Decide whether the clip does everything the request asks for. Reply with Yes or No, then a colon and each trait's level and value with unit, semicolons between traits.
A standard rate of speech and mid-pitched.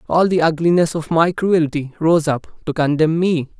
Yes: average, 185 wpm; medium, 160 Hz